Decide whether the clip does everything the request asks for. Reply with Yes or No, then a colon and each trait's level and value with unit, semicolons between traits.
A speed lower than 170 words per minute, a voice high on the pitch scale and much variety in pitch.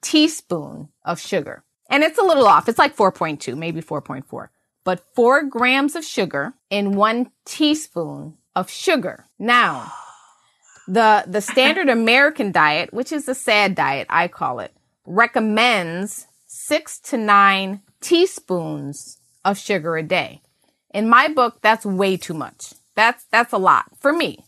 Yes: average, 145 wpm; high, 215 Hz; wide, 6.2 semitones